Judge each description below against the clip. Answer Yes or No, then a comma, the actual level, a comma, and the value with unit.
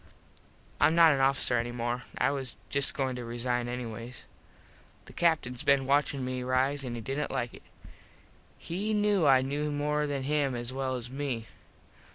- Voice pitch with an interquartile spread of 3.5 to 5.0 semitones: No, average, 2.9 semitones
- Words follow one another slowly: No, average, 175 wpm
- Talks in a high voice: No, low, 135 Hz